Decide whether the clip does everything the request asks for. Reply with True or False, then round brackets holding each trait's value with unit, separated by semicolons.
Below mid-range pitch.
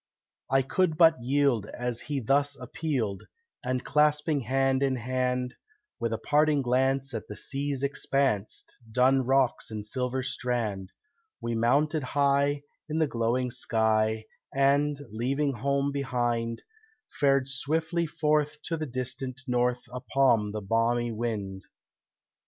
True (130 Hz)